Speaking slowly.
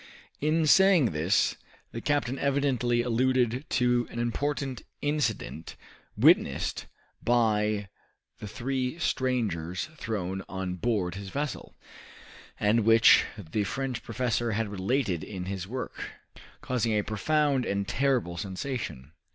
Yes: slow, 115 wpm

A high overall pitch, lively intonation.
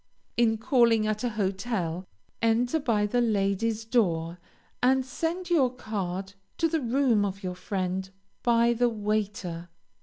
No: high, 220 Hz; average, 3.9 semitones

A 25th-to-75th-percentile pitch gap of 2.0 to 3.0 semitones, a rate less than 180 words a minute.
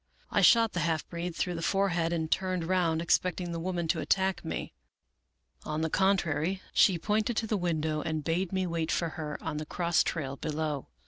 No: average, 2.7 semitones; average, 195 wpm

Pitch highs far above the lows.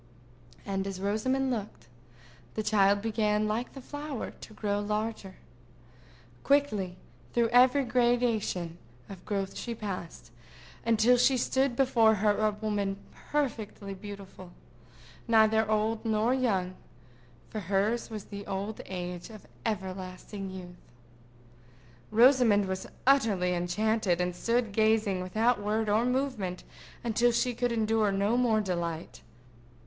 No: average, 3.3 semitones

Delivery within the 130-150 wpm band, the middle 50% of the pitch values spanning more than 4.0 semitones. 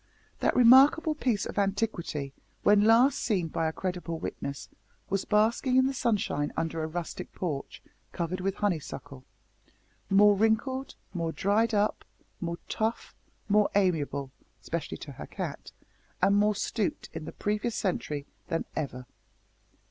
Yes: average, 140 wpm; average, 5.1 semitones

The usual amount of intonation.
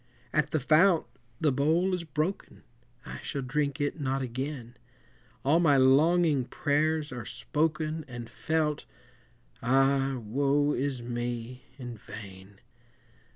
Yes: average, 3.8 semitones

